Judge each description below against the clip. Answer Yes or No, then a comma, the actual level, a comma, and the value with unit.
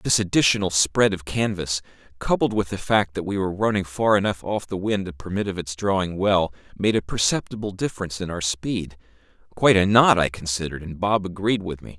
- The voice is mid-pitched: No, very low, 95 Hz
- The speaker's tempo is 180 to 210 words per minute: Yes, average, 200 wpm